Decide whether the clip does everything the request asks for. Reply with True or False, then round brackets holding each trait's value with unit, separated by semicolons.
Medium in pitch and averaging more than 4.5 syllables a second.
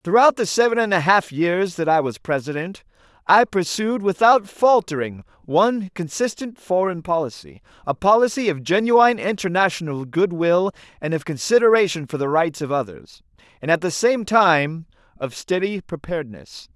True (175 Hz; 5.0 syllables/s)